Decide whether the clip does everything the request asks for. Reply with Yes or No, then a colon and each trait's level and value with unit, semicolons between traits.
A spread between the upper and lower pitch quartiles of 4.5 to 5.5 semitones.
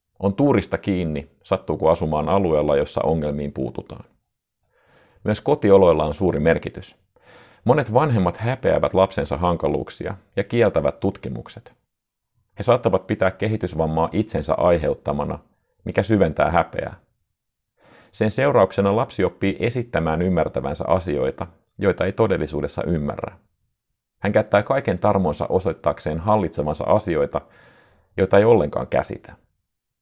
Yes: average, 5.0 semitones